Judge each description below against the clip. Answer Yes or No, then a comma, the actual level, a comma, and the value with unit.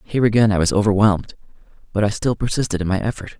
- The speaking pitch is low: Yes, low, 105 Hz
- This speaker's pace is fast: Yes, fast, 210 wpm